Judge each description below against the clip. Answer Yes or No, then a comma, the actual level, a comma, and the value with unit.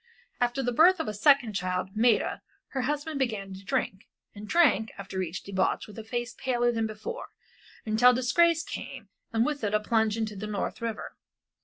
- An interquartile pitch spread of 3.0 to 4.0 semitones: Yes, average, 3.7 semitones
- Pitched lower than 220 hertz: No, high, 225 Hz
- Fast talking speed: No, average, 185 wpm